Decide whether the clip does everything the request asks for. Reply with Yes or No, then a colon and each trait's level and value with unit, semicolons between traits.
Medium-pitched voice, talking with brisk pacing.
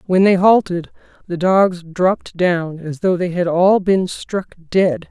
No: medium, 180 Hz; average, 175 wpm